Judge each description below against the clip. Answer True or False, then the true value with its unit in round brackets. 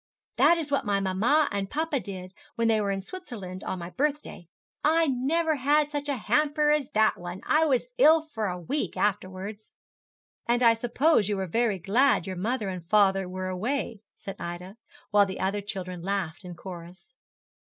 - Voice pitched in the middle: False (210 Hz)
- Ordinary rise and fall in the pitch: False (7.0 semitones)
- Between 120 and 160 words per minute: False (185 wpm)